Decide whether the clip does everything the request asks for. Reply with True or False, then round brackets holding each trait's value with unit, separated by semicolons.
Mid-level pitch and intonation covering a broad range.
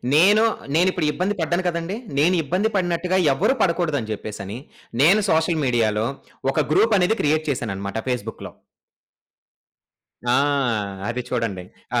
True (160 Hz; 7.3 semitones)